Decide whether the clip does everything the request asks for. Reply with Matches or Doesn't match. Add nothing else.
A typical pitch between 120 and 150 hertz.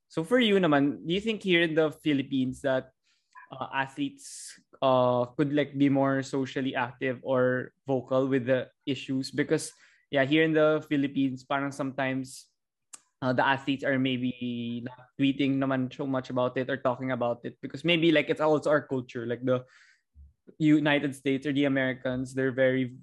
Matches